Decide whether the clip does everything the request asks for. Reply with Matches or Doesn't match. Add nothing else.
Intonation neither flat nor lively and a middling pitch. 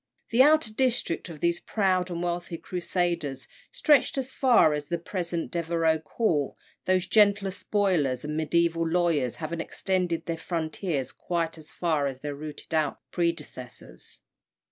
Matches